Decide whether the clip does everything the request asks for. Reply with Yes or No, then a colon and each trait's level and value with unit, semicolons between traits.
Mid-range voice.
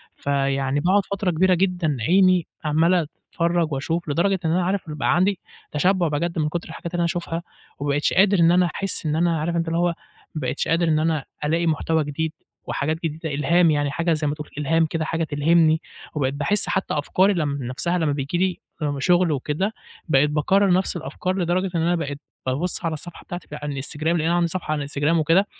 Yes: medium, 165 Hz